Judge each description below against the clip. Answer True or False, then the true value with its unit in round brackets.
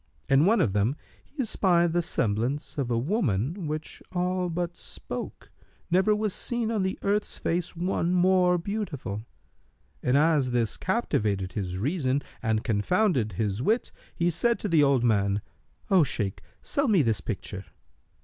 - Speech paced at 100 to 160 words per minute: True (155 wpm)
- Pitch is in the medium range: True (160 Hz)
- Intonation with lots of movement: True (8.4 semitones)